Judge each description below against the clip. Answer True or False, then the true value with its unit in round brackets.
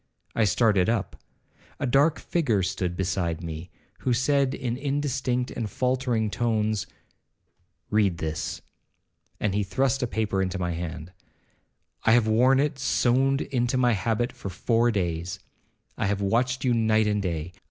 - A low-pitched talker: True (110 Hz)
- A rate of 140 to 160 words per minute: True (150 wpm)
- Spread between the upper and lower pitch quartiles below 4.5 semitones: False (5.0 semitones)